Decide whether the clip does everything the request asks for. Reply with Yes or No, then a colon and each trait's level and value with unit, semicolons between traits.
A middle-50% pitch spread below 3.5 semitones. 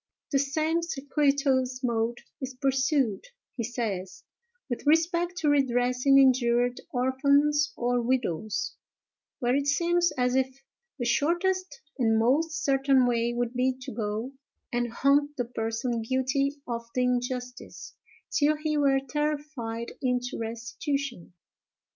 Yes: average, 3.0 semitones